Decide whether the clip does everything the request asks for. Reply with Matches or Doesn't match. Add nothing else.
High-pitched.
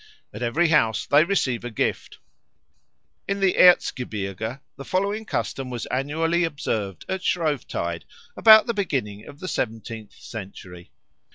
Doesn't match